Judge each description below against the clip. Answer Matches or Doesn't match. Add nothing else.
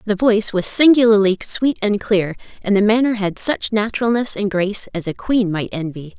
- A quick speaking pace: Doesn't match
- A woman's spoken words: Matches